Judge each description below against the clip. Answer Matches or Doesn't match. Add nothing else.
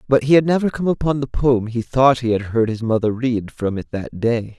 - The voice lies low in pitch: Matches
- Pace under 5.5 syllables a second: Matches